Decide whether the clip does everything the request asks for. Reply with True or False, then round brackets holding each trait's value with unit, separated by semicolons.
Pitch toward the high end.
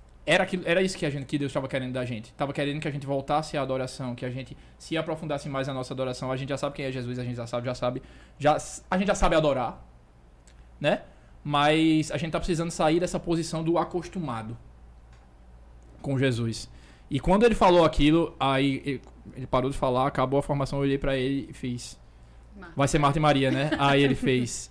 False (140 Hz)